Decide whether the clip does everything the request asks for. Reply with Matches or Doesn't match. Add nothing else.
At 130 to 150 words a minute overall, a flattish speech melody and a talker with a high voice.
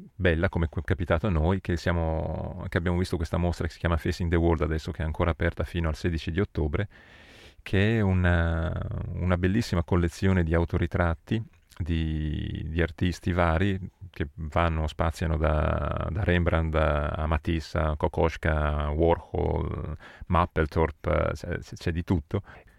Doesn't match